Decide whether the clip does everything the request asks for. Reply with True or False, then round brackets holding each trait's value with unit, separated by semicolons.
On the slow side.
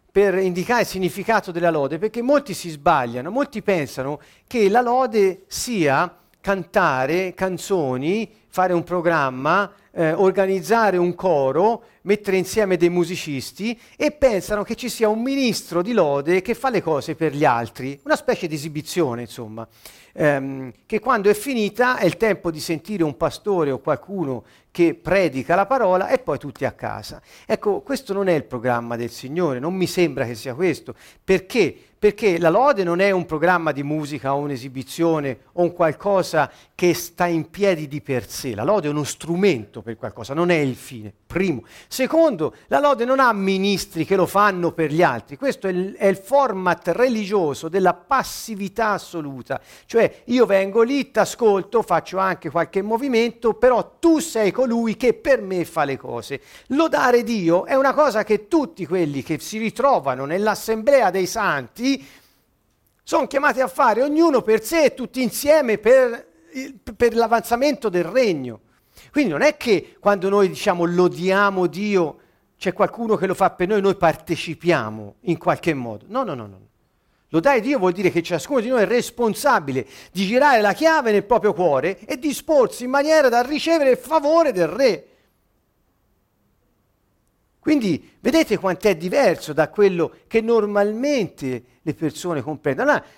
False (165 wpm)